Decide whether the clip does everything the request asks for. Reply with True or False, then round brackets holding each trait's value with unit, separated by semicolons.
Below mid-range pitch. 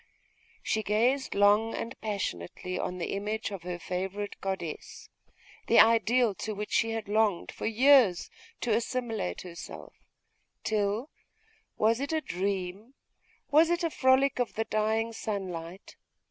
False (215 Hz)